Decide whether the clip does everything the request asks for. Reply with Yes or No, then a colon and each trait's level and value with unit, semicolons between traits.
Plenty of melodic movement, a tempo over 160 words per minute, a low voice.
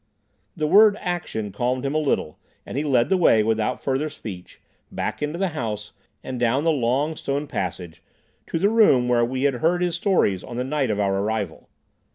Yes: wide, 5.8 semitones; average, 200 wpm; low, 130 Hz